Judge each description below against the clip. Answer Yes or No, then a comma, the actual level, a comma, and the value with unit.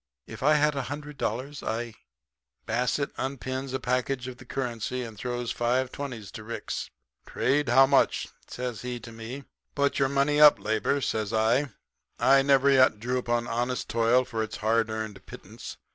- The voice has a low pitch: Yes, low, 125 Hz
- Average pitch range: Yes, average, 3.1 semitones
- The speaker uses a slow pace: No, average, 175 wpm